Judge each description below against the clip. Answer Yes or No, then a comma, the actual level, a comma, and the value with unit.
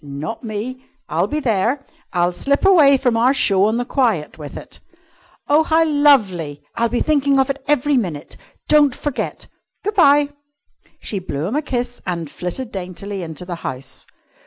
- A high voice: Yes, high, 240 Hz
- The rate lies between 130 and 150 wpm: No, average, 170 wpm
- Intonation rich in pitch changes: Yes, wide, 7.8 semitones